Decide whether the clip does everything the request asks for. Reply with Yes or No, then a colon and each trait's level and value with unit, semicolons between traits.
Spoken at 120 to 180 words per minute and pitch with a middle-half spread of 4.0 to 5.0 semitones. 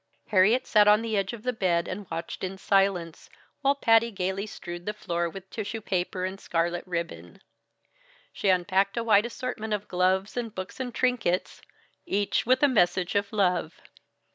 No: average, 170 wpm; average, 3.4 semitones